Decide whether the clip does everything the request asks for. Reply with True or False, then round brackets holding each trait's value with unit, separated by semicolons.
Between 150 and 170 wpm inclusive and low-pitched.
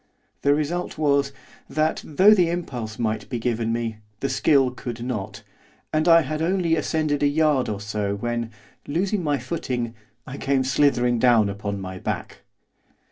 True (160 wpm; 130 Hz)